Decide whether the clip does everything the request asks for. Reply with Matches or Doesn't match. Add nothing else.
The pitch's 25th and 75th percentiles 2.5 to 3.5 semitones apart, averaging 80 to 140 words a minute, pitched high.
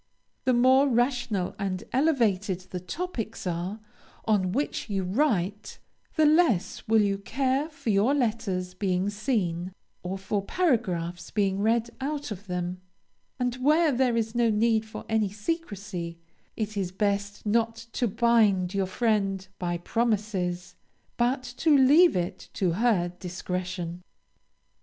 Doesn't match